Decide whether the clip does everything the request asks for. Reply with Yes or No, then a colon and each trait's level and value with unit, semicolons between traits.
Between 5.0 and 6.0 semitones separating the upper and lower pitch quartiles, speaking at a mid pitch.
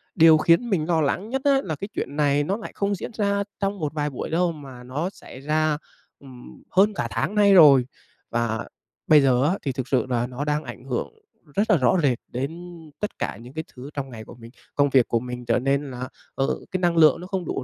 Yes: wide, 5.5 semitones; medium, 150 Hz